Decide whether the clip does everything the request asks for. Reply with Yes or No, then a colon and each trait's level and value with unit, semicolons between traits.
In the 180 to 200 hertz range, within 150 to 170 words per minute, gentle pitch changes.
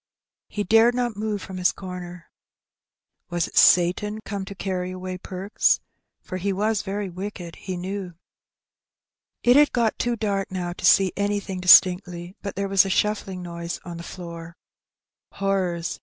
Yes: high, 190 Hz; average, 155 wpm; narrow, 2.3 semitones